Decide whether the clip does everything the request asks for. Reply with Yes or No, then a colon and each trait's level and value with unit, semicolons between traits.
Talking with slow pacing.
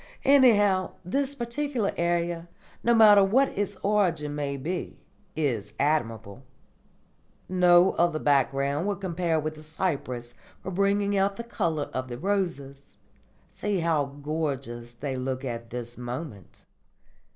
Yes: slow, 130 wpm